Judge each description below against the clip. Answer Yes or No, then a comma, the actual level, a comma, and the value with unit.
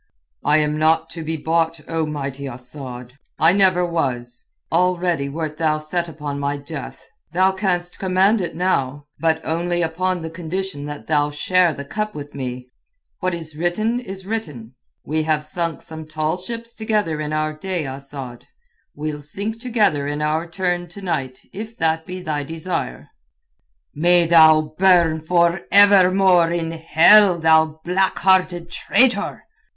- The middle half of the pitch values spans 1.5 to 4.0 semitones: Yes, average, 3.4 semitones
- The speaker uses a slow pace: No, average, 155 wpm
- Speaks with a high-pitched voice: No, medium, 165 Hz